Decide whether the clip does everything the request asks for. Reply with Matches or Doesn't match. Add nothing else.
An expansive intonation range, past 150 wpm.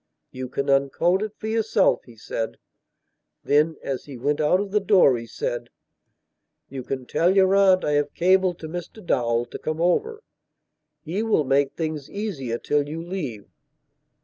Matches